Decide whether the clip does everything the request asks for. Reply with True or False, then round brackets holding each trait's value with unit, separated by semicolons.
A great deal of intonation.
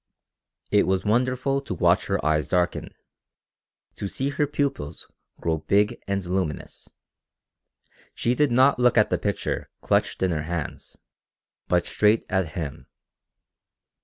True (6.3 semitones)